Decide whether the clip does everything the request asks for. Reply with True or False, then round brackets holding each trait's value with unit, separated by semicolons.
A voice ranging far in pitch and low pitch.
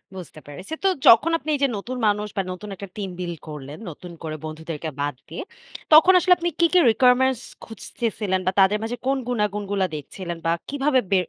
False (6.9 semitones; 205 Hz)